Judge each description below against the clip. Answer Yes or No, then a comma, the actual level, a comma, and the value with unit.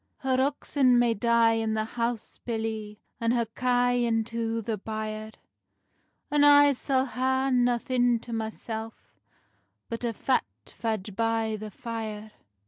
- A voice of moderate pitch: No, high, 230 Hz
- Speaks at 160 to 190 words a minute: No, slow, 135 wpm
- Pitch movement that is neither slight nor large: No, narrow, 2.0 semitones